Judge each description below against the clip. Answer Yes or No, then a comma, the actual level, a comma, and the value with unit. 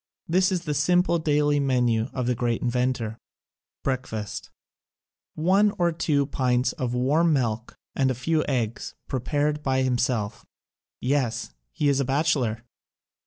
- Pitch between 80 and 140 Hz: Yes, low, 135 Hz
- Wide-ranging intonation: No, average, 3.6 semitones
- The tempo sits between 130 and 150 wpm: Yes, average, 140 wpm